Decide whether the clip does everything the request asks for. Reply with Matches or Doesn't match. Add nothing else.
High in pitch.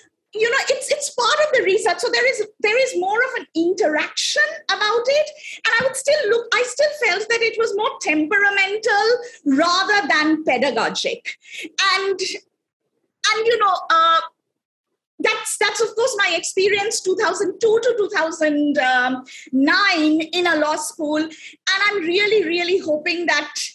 Matches